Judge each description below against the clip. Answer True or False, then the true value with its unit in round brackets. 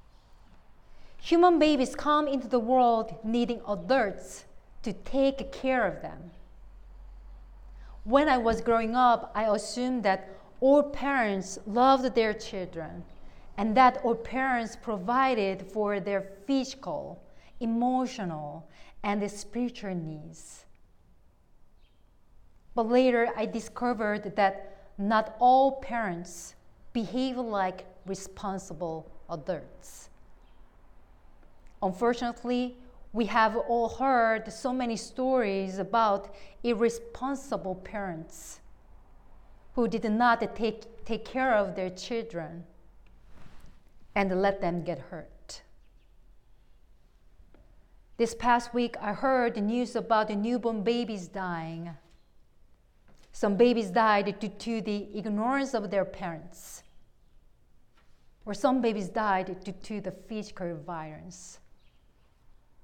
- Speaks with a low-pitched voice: False (220 Hz)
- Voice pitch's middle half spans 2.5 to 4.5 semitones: True (3.9 semitones)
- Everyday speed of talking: False (100 wpm)